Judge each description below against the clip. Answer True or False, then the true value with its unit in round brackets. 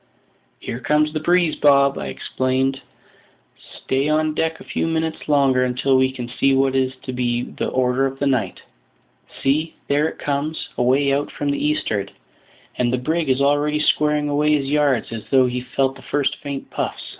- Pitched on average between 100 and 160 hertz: True (140 Hz)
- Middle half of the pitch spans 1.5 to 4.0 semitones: True (2.5 semitones)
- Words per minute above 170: True (185 wpm)